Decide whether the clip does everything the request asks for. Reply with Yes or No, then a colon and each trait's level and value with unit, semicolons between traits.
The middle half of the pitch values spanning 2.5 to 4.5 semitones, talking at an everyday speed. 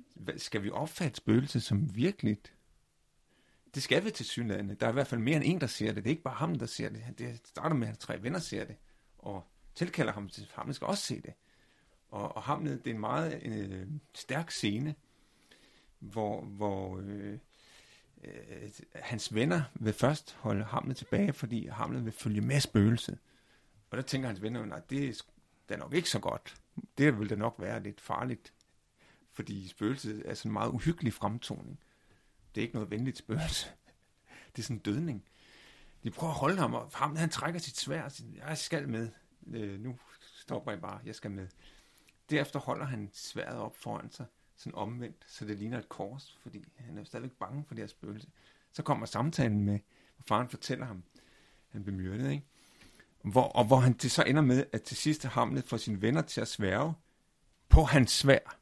No: average, 5.0 semitones; average, 195 wpm